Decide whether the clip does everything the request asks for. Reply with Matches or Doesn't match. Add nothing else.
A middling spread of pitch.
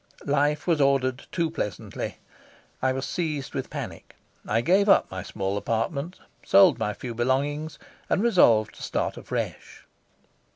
Doesn't match